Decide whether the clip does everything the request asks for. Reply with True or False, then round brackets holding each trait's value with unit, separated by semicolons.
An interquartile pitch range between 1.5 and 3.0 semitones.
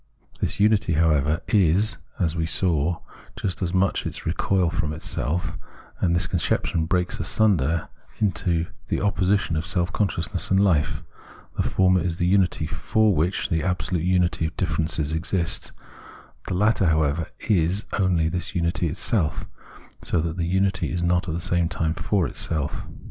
True (2.6 semitones)